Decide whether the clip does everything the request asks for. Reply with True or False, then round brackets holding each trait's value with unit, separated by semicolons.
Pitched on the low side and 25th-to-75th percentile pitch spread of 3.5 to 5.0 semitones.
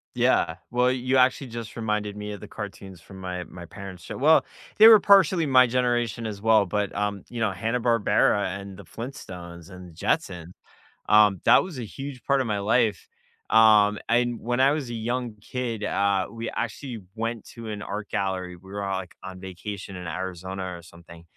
True (105 Hz; 4.1 semitones)